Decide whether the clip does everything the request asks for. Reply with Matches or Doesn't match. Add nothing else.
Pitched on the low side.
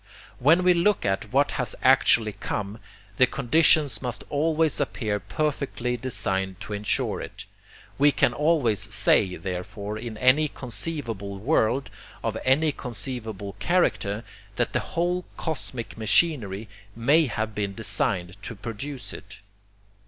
Matches